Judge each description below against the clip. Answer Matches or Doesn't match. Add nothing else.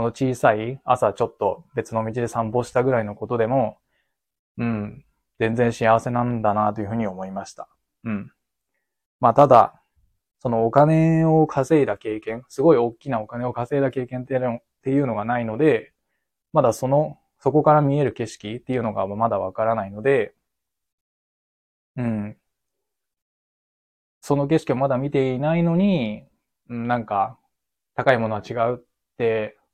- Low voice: Matches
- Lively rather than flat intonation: Doesn't match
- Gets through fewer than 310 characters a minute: Matches